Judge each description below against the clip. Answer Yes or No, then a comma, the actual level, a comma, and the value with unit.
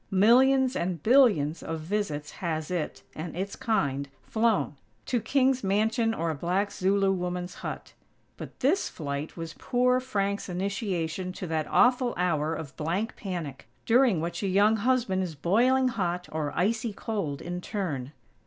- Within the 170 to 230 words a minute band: No, average, 155 wpm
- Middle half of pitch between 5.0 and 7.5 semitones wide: Yes, wide, 5.5 semitones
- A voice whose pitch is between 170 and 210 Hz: Yes, high, 190 Hz